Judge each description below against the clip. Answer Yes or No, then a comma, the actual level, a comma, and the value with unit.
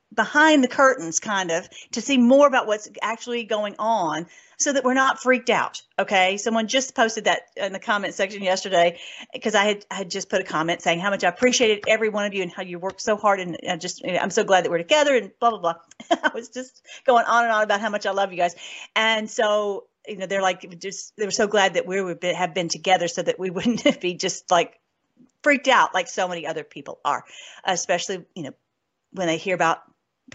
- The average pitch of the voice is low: No, high, 200 Hz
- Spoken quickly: Yes, fast, 240 wpm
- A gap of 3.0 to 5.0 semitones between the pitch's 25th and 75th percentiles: Yes, average, 4.3 semitones